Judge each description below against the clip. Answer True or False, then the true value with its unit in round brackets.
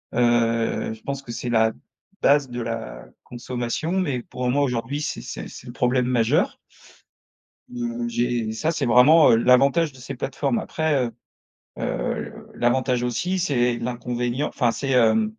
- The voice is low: True (125 Hz)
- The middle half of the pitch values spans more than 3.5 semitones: False (3.2 semitones)